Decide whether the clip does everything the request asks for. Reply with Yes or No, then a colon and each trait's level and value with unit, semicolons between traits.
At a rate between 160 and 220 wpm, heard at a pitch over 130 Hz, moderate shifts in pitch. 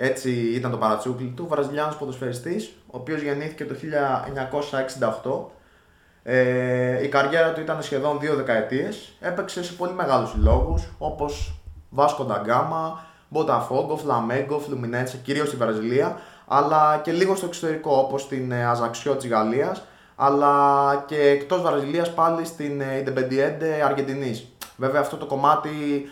No: average, 130 wpm; medium, 140 Hz; average, 3.1 semitones